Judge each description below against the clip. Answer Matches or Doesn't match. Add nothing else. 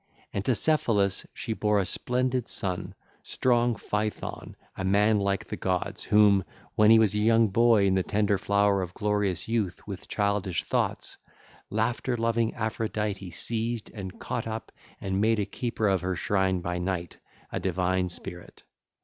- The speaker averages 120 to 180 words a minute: Matches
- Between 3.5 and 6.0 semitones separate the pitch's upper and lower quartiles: Doesn't match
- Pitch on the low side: Matches